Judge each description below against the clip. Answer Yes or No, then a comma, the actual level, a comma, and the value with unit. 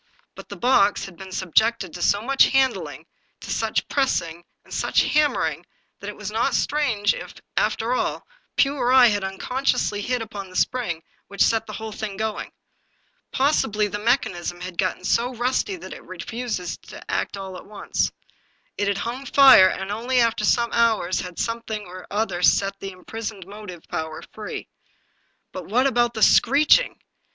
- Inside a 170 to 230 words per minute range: Yes, average, 175 wpm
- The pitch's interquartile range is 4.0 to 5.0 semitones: Yes, average, 4.3 semitones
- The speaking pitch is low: No, high, 215 Hz